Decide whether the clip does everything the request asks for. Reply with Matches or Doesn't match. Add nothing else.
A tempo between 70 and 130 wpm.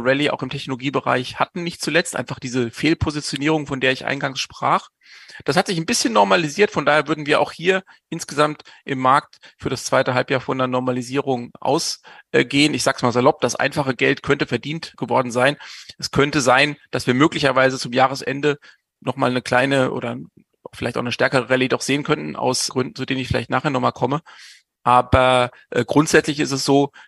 Doesn't match